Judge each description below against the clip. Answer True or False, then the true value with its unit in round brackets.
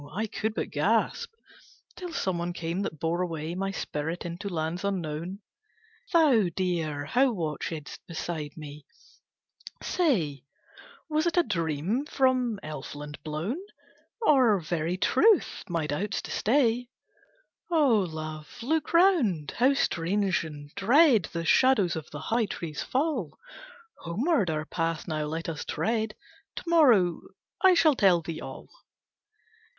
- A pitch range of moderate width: False (7.7 semitones)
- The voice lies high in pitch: False (180 Hz)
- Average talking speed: False (130 wpm)